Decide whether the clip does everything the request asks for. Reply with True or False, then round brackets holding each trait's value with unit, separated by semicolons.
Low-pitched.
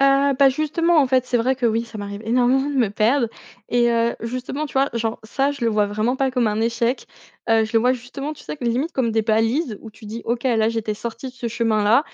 False (235 Hz)